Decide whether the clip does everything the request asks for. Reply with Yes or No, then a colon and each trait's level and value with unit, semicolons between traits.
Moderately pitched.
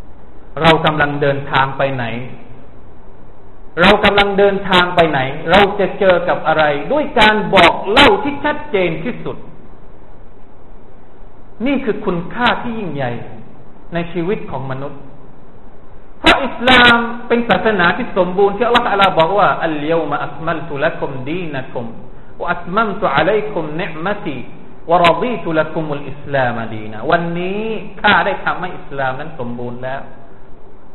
Yes: medium, 170 Hz